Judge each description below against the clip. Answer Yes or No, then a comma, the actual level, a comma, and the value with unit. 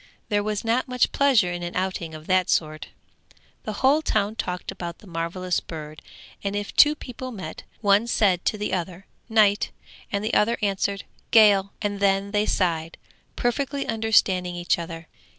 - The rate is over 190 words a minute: No, average, 170 wpm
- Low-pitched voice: No, high, 200 Hz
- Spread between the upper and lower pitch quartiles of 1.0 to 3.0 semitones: No, average, 3.7 semitones